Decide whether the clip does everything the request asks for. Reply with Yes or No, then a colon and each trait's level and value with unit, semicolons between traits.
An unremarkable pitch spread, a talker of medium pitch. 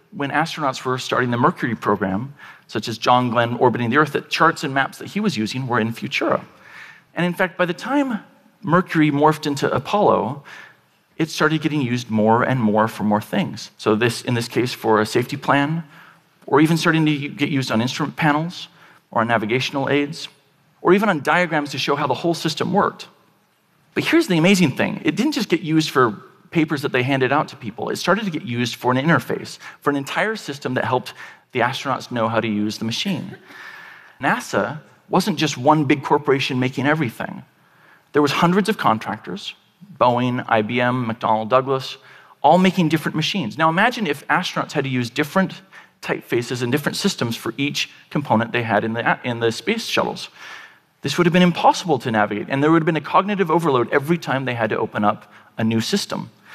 No: wide, 5.8 semitones; medium, 145 Hz